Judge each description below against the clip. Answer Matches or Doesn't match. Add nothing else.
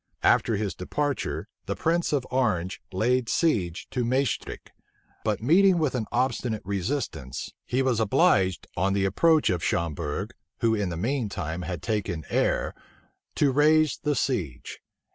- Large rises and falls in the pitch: Matches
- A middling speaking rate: Matches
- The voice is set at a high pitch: Doesn't match